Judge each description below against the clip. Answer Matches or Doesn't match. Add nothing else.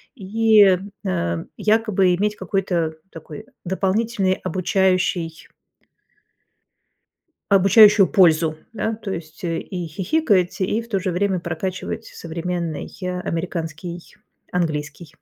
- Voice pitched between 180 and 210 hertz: Matches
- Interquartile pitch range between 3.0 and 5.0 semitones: Matches